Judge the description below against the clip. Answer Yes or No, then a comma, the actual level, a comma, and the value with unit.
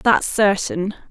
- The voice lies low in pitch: No, high, 205 Hz